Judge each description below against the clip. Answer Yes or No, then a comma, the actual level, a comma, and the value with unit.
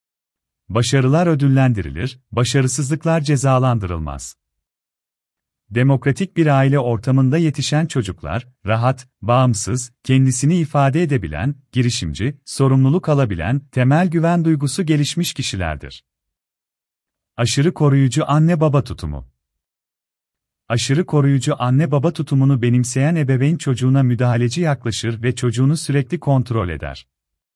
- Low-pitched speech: Yes, low, 130 Hz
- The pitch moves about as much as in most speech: No, wide, 6.1 semitones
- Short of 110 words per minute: Yes, slow, 95 wpm